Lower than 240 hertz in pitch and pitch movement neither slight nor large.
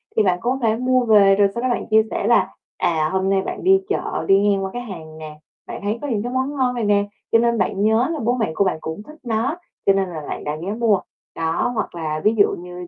Yes: high, 210 Hz; average, 4.6 semitones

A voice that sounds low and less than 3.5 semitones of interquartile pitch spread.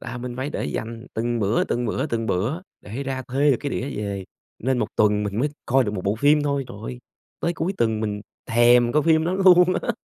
No: low, 120 Hz; average, 4.6 semitones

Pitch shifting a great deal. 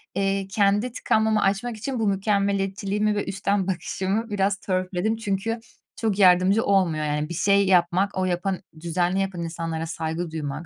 No: narrow, 2.5 semitones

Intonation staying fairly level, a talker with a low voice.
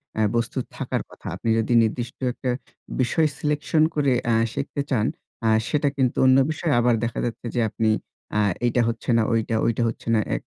No: average, 3.6 semitones; low, 120 Hz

